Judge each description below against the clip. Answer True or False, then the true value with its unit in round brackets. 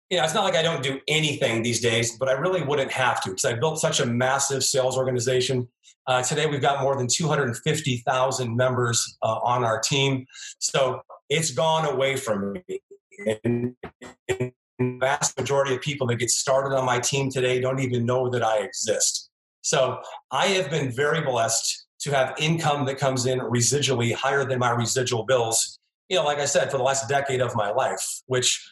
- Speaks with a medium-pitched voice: False (130 Hz)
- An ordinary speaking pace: True (195 wpm)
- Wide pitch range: False (2.5 semitones)